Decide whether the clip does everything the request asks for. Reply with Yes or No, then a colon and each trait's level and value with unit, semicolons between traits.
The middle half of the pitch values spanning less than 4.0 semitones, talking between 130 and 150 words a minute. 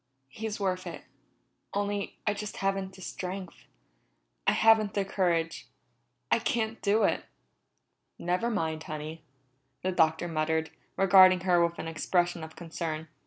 Yes: average, 3.6 semitones; slow, 135 wpm